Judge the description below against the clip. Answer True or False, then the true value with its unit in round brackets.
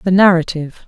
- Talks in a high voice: False (175 Hz)